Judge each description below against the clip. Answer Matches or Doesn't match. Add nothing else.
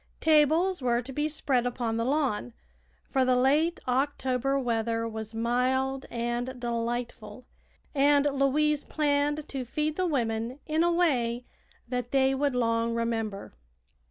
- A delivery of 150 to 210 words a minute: Doesn't match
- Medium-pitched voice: Doesn't match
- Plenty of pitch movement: Doesn't match